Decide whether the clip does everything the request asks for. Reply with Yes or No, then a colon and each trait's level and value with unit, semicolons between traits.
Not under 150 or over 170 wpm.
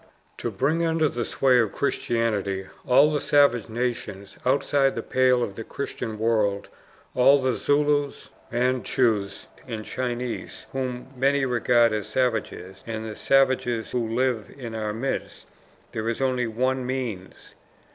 No: average, 140 wpm